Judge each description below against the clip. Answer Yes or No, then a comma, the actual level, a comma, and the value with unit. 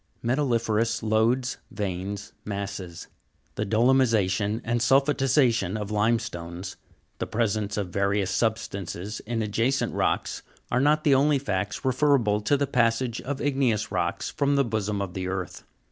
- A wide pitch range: No, average, 4.4 semitones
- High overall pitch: No, low, 110 Hz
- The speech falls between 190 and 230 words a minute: No, average, 145 wpm